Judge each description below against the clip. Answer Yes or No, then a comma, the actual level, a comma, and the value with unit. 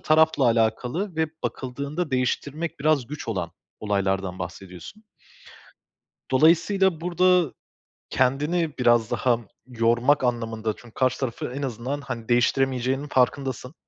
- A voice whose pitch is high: No, low, 130 Hz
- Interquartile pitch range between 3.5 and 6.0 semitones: Yes, average, 4.7 semitones